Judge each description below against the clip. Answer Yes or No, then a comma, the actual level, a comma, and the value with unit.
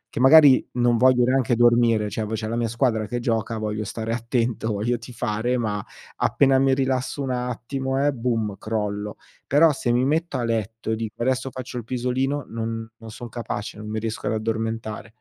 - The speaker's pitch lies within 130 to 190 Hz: No, low, 120 Hz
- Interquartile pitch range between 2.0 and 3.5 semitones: Yes, narrow, 2.6 semitones